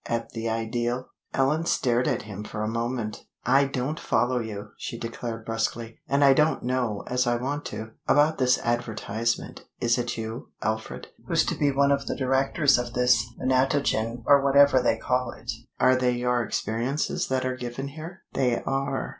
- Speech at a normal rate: Yes, average, 180 wpm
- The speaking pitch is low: Yes, low, 125 Hz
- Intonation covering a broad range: No, average, 2.7 semitones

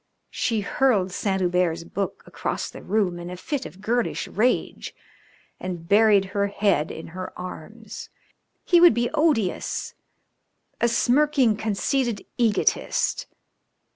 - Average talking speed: No, slow, 125 wpm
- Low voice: No, high, 205 Hz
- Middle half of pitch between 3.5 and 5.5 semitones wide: Yes, average, 4.6 semitones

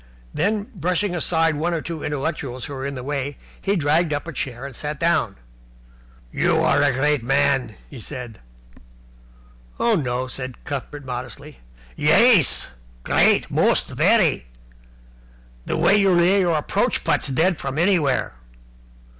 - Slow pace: No, average, 145 wpm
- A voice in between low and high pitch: Yes, medium, 145 Hz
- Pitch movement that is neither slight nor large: Yes, average, 4.5 semitones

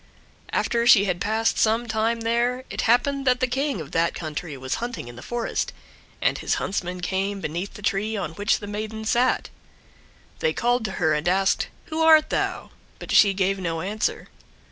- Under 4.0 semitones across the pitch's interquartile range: No, average, 4.7 semitones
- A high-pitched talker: Yes, high, 215 Hz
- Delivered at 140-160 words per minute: No, average, 190 wpm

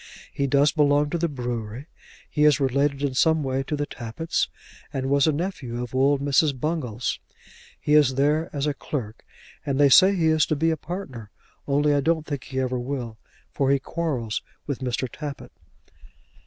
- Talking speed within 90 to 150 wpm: No, average, 185 wpm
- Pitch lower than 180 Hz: Yes, medium, 140 Hz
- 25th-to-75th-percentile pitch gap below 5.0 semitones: Yes, narrow, 2.6 semitones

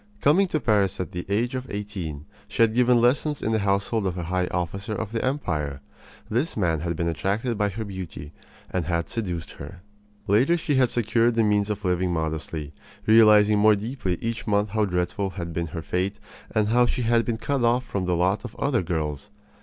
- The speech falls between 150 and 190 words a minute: No, fast, 205 wpm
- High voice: No, low, 105 Hz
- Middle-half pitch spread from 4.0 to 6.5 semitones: Yes, average, 4.6 semitones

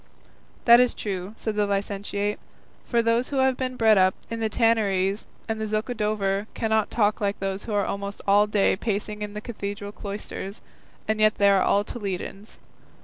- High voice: Yes, high, 210 Hz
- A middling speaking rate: Yes, average, 175 wpm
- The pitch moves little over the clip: Yes, narrow, 1.8 semitones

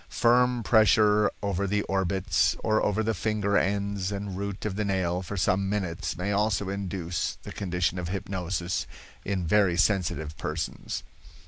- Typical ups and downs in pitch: No, narrow, 2.2 semitones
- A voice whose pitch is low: Yes, low, 100 Hz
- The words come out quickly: No, average, 150 wpm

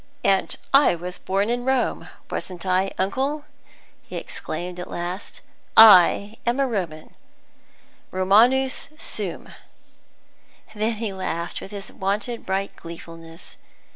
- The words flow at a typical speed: No, slow, 115 wpm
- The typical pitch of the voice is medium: No, high, 195 Hz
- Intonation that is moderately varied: Yes, average, 4.5 semitones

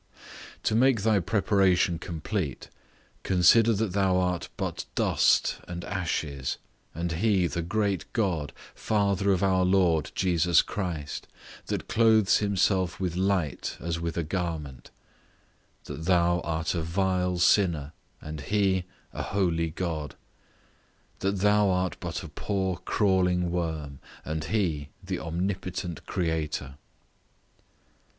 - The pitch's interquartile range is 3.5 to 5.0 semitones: No, average, 3.0 semitones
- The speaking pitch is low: Yes, very low, 90 Hz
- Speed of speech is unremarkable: No, slow, 120 wpm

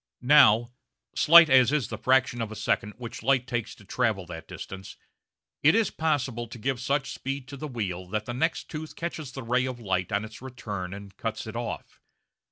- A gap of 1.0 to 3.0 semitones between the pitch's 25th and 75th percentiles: No, average, 4.1 semitones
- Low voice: Yes, low, 120 Hz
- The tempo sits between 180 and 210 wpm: Yes, average, 200 wpm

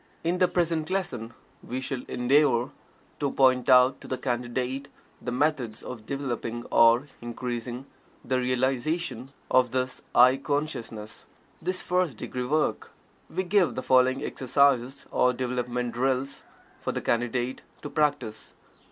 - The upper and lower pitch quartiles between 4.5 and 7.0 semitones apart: No, average, 2.7 semitones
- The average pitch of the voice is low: Yes, low, 130 Hz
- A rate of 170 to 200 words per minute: No, slow, 135 wpm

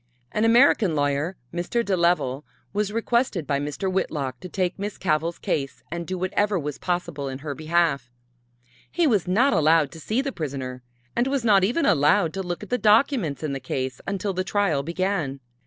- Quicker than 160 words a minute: Yes, average, 190 wpm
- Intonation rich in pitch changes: Yes, wide, 5.9 semitones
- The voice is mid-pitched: Yes, medium, 175 Hz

